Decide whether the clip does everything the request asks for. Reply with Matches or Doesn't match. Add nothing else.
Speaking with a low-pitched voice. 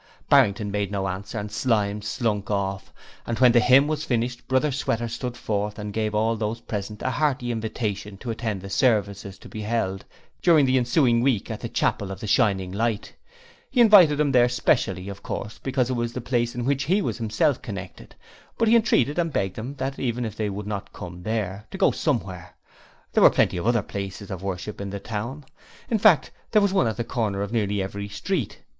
Matches